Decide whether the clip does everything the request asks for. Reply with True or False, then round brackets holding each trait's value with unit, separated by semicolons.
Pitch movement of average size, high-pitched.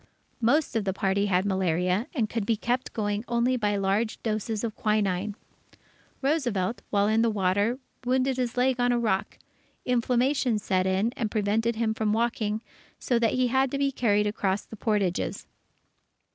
True (3.1 semitones; 220 Hz)